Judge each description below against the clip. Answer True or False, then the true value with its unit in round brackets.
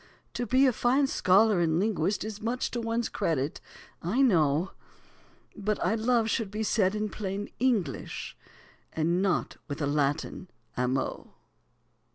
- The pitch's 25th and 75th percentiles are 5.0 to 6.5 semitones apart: True (5.6 semitones)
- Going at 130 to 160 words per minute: True (145 wpm)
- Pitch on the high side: True (205 Hz)